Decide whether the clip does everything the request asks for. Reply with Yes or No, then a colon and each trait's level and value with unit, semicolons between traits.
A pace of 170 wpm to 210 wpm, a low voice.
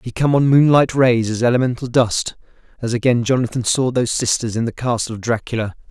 Yes: average, 185 wpm; low, 120 Hz